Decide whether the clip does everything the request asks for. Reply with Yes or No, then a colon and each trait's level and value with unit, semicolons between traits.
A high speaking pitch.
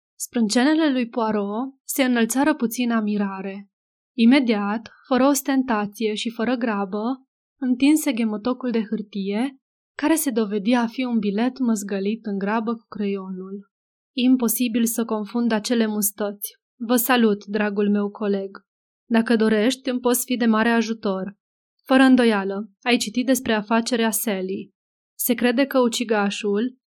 Yes: high, 230 Hz